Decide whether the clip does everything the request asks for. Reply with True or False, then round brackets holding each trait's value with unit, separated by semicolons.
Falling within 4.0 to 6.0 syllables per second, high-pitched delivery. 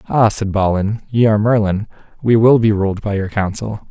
False (5.3 syllables/s; 105 Hz)